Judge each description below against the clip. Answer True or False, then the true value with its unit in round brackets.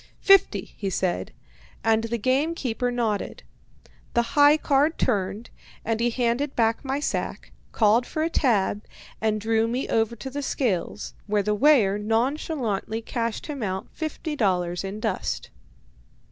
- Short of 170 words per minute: True (145 wpm)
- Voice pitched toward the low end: False (230 Hz)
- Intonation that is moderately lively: True (4.4 semitones)